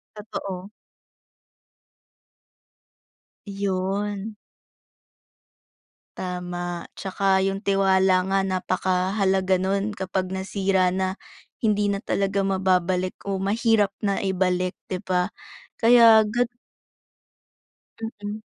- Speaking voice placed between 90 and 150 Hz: No, high, 195 Hz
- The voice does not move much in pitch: Yes, narrow, 1.5 semitones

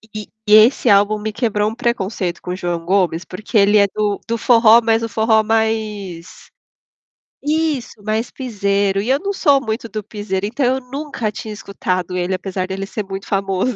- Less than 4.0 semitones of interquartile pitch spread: Yes, average, 2.8 semitones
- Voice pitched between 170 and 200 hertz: No, high, 215 Hz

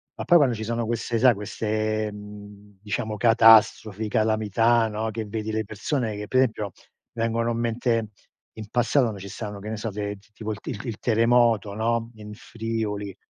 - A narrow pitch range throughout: Yes, narrow, 1.8 semitones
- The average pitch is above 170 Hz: No, low, 110 Hz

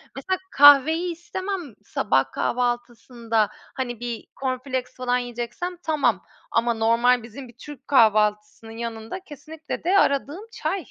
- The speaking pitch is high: Yes, very high, 250 Hz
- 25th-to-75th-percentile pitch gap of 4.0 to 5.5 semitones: Yes, average, 4.3 semitones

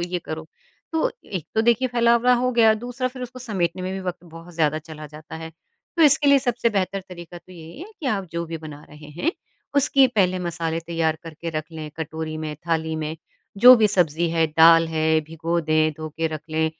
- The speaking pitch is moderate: Yes, medium, 170 Hz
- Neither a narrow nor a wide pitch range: No, wide, 5.8 semitones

